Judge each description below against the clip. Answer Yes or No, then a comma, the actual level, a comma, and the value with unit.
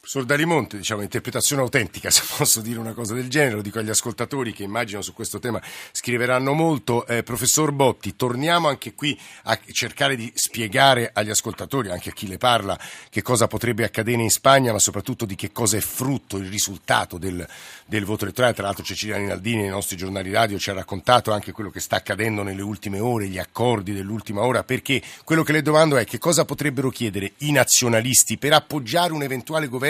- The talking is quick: Yes, fast, 195 wpm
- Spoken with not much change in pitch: No, average, 4.3 semitones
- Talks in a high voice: No, low, 115 Hz